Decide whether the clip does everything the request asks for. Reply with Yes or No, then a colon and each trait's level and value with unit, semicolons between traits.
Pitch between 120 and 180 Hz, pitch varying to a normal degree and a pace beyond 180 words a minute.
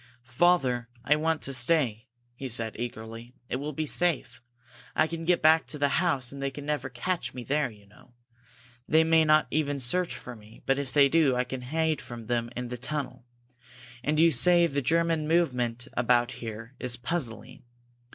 Yes: low, 135 Hz; average, 4.6 semitones; average, 190 wpm